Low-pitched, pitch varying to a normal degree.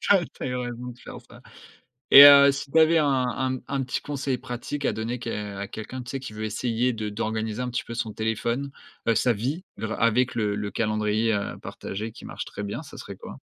Yes: low, 120 Hz; average, 3.3 semitones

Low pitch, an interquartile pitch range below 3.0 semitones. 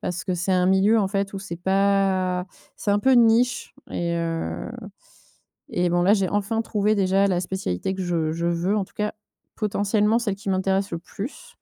No: high, 195 Hz; narrow, 2.5 semitones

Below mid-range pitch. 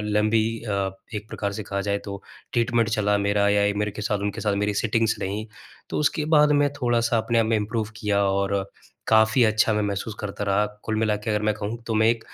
Yes: low, 105 Hz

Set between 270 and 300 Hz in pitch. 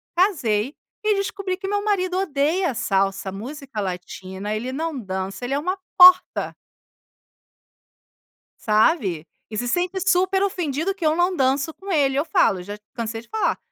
Yes: very high, 285 Hz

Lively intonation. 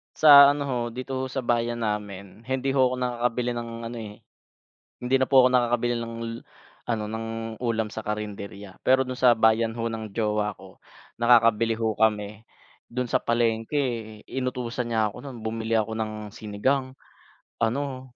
No: narrow, 2.4 semitones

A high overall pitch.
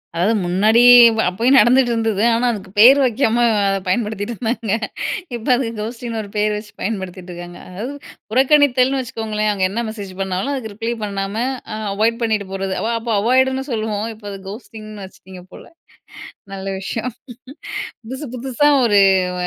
Yes: high, 220 Hz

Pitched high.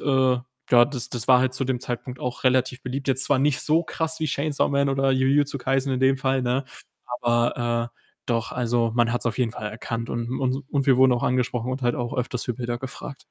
No: low, 130 Hz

